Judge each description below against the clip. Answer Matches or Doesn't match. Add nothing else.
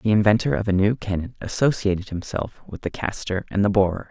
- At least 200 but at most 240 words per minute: Matches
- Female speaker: Doesn't match